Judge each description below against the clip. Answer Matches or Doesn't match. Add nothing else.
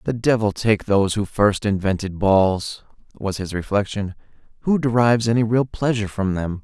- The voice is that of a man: Matches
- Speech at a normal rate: Matches